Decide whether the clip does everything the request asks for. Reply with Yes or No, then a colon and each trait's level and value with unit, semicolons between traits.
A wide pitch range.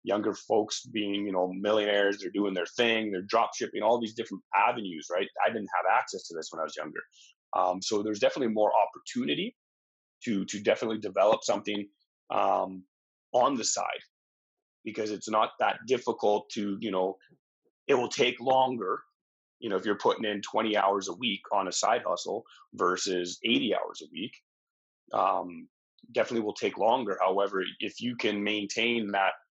No: average, 2.8 semitones